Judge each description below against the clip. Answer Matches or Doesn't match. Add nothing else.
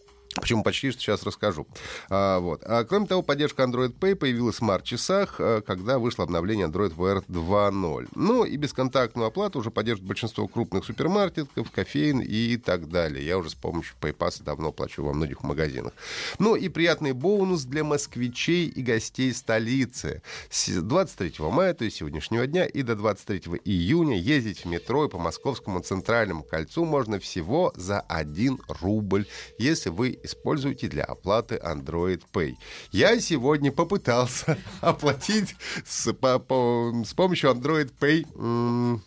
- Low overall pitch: Matches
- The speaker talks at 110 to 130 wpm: Doesn't match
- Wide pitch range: Matches